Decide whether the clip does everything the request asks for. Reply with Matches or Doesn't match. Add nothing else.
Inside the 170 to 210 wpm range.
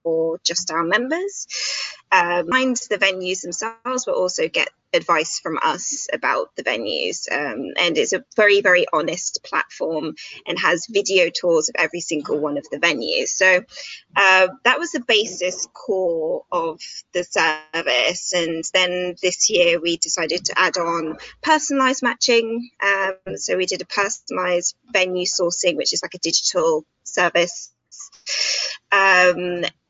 Doesn't match